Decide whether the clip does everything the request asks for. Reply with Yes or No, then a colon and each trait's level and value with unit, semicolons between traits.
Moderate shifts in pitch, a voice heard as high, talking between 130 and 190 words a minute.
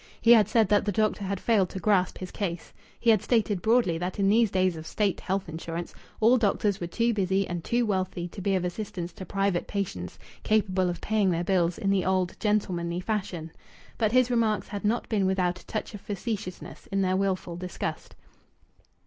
No: average, 3.0 semitones; high, 195 Hz; average, 200 wpm